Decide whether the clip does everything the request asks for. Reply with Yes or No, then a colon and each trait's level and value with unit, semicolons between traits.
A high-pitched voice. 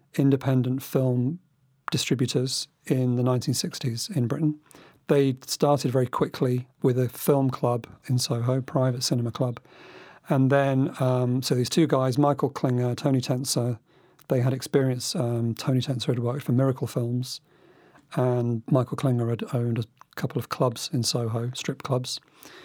No: low, 130 Hz